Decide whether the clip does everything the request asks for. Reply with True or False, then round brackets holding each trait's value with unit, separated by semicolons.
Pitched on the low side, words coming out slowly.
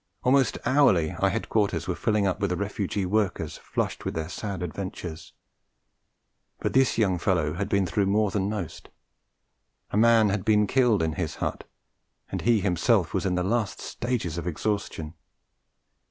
False (100 Hz; 160 wpm)